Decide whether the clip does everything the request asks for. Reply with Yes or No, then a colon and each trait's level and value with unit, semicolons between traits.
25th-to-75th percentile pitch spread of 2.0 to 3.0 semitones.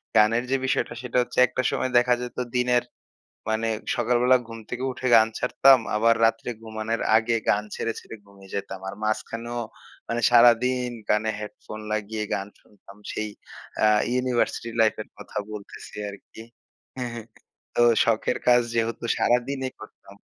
Yes: narrow, 2.4 semitones